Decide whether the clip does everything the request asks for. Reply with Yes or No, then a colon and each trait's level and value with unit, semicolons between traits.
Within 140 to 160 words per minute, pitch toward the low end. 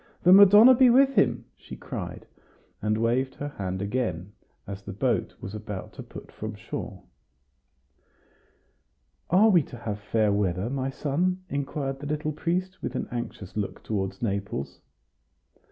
Yes: average, 150 wpm; low, 125 Hz